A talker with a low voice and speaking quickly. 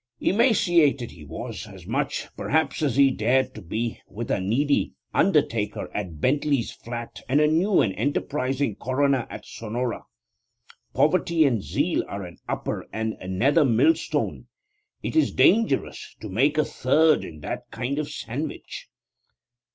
No: low, 130 Hz; average, 145 wpm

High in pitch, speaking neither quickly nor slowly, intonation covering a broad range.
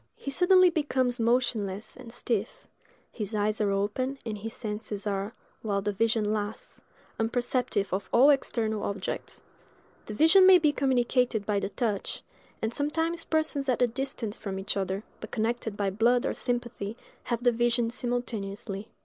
No: high, 230 Hz; average, 160 wpm; average, 3.5 semitones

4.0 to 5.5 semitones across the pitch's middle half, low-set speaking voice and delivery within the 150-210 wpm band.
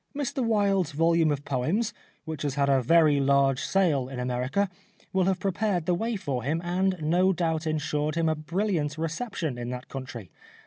No: average, 5.2 semitones; medium, 160 Hz; average, 180 wpm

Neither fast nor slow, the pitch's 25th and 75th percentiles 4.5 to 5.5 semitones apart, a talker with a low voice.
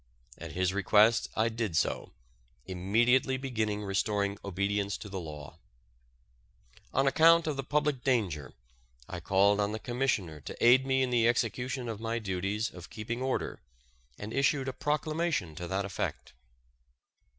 Yes: average, 150 wpm; average, 4.9 semitones; low, 110 Hz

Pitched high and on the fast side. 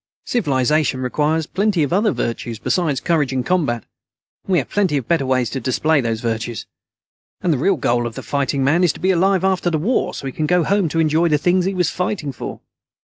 No: medium, 155 Hz; fast, 225 wpm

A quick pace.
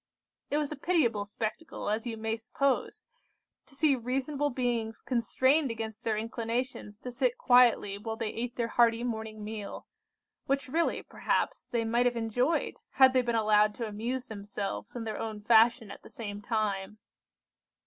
No: average, 165 wpm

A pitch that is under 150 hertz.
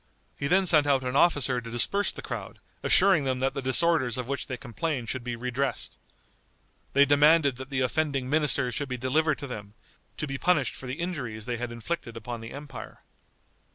Yes: low, 135 Hz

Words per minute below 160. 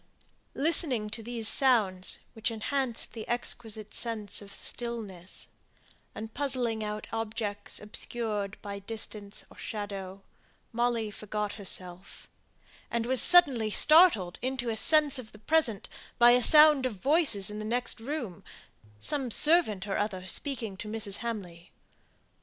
Yes: slow, 135 wpm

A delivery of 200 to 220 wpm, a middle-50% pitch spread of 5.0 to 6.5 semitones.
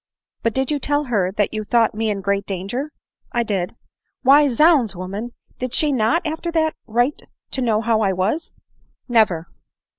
Yes: fast, 205 wpm; wide, 5.4 semitones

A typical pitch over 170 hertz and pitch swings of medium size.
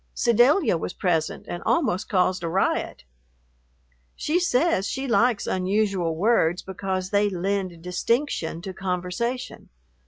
Yes: high, 190 Hz; average, 4.7 semitones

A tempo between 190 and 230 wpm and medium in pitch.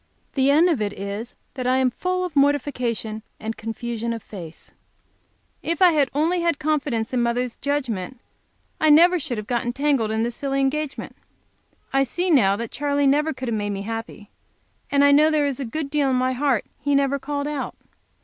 No: average, 195 wpm; very high, 270 Hz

